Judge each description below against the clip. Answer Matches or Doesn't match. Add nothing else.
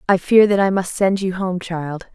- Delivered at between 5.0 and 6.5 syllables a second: Doesn't match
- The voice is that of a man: Doesn't match